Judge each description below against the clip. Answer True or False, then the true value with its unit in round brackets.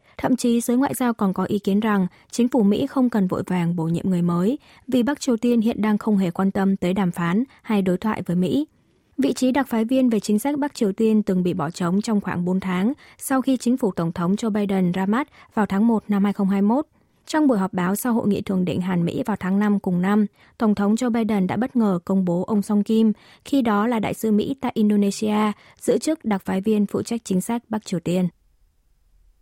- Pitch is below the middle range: False (210 Hz)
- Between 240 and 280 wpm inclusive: True (245 wpm)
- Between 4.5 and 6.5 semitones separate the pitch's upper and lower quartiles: False (3.9 semitones)